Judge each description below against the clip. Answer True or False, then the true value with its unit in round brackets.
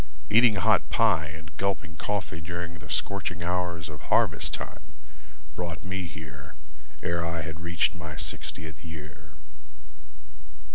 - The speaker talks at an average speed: False (130 wpm)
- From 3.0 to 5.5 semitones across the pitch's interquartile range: False (2.6 semitones)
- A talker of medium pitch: False (85 Hz)